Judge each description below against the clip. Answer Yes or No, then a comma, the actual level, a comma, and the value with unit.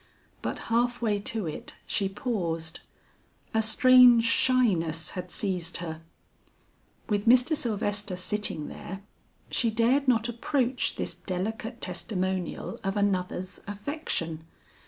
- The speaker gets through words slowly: Yes, slow, 115 wpm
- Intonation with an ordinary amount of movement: Yes, average, 4.6 semitones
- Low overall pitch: No, high, 205 Hz